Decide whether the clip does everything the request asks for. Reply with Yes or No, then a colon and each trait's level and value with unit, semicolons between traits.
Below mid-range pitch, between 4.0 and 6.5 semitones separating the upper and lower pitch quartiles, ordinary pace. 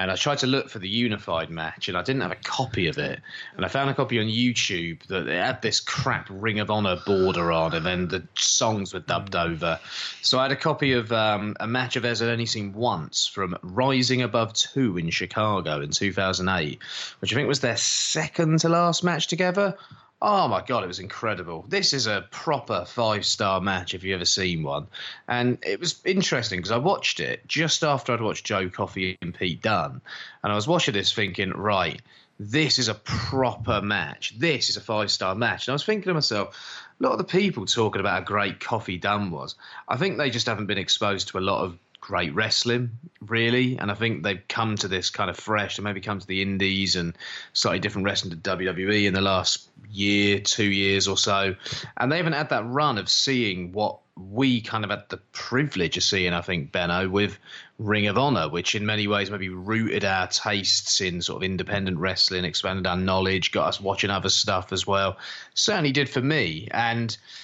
No: low, 105 Hz; average, 4.6 semitones; fast, 215 wpm